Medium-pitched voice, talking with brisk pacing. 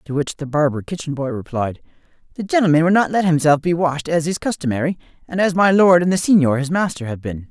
Yes: medium, 160 Hz; fast, 230 wpm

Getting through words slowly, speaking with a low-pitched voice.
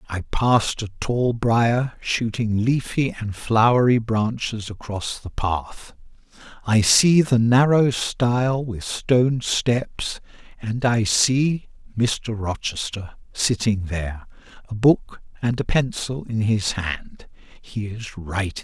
Yes: slow, 120 wpm; low, 115 Hz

